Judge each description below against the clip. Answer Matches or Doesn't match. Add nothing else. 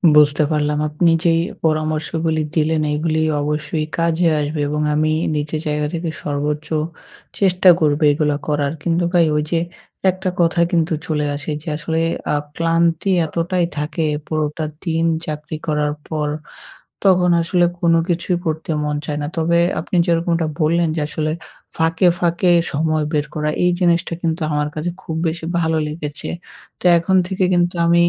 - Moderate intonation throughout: Doesn't match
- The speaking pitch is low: Doesn't match